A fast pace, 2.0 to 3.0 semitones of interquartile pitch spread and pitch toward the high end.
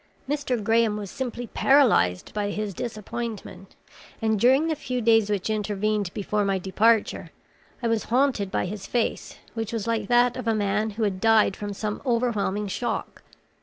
No: average, 165 wpm; narrow, 2.5 semitones; high, 215 Hz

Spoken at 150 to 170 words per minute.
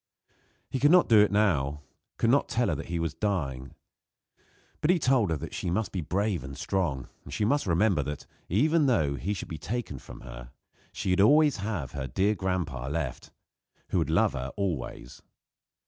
No: average, 185 wpm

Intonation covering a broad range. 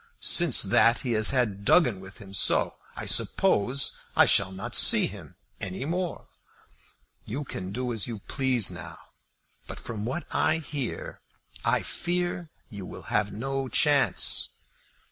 Yes: wide, 5.7 semitones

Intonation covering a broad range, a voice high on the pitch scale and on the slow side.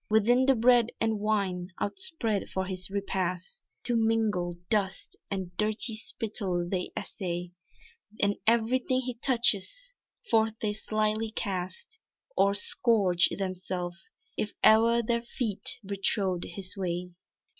No: average, 3.6 semitones; high, 210 Hz; slow, 120 wpm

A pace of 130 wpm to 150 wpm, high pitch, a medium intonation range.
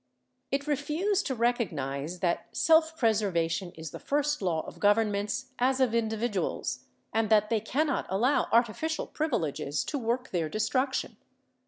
No: average, 140 wpm; high, 225 Hz; wide, 5.9 semitones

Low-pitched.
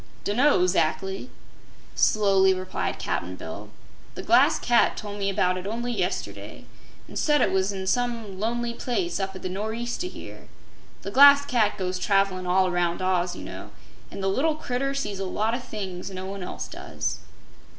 No: high, 195 Hz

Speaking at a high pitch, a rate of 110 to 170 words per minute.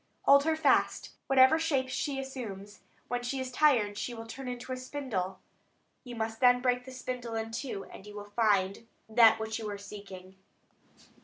No: high, 240 Hz; average, 180 wpm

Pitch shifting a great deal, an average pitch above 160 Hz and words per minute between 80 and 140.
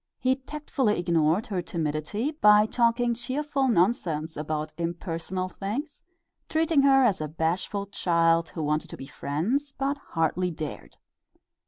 Yes: wide, 8.0 semitones; high, 190 Hz; slow, 135 wpm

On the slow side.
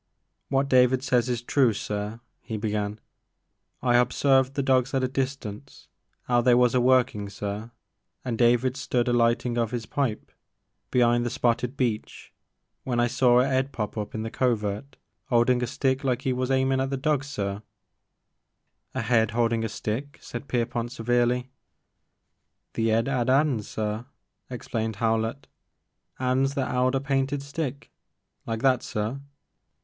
No: average, 165 wpm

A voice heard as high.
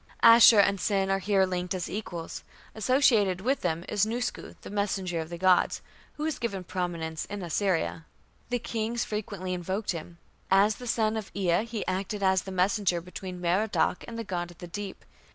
Yes: high, 195 Hz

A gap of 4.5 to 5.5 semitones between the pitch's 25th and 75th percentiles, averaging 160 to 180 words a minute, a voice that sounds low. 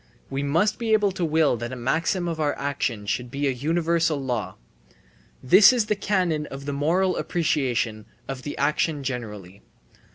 No: average, 5.0 semitones; average, 170 wpm; medium, 145 Hz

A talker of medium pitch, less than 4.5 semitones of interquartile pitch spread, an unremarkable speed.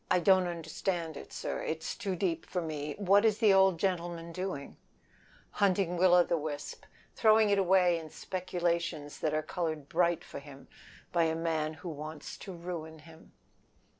Yes: medium, 170 Hz; average, 2.8 semitones; average, 165 wpm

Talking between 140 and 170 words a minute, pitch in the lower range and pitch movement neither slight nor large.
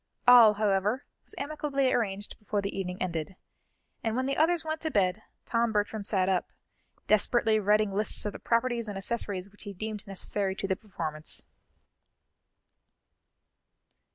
No: average, 150 wpm; high, 210 Hz; average, 3.4 semitones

